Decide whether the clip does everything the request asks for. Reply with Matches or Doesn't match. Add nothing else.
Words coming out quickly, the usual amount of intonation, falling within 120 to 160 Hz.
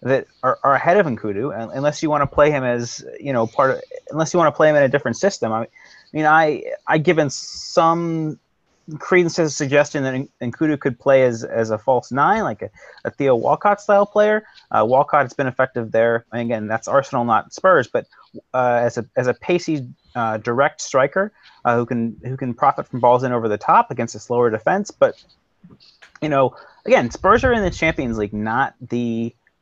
Matches